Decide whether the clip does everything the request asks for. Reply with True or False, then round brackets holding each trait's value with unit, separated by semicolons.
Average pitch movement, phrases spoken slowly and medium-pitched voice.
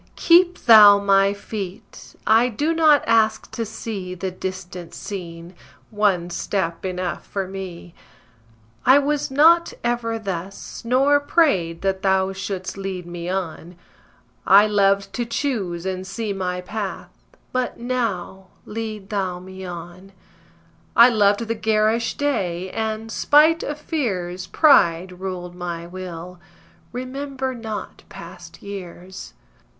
False (4.1 semitones; 125 wpm; 195 Hz)